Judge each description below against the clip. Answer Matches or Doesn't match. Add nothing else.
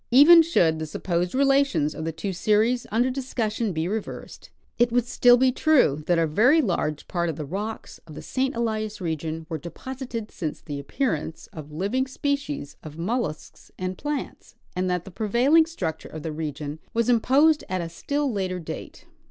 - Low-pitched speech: Doesn't match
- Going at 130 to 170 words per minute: Doesn't match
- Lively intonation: Matches